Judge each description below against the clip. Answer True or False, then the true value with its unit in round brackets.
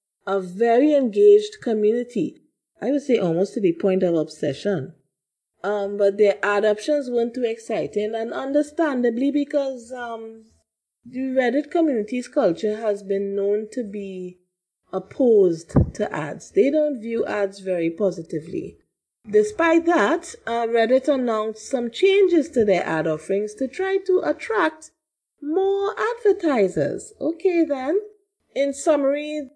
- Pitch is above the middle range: True (240 Hz)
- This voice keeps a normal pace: False (130 wpm)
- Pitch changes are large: True (6.9 semitones)